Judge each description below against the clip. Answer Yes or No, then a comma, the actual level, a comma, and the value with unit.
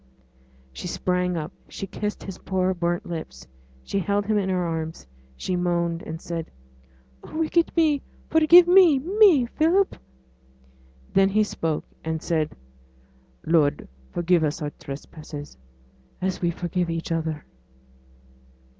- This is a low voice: No, medium, 180 Hz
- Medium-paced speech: No, slow, 130 wpm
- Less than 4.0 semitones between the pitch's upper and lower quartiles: No, average, 4.7 semitones